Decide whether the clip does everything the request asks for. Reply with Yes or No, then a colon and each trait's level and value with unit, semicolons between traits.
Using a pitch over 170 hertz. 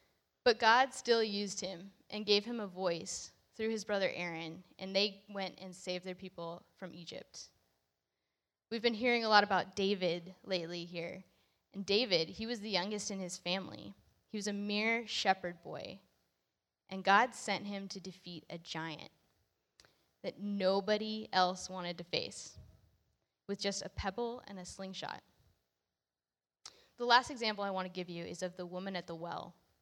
Yes: medium, 185 Hz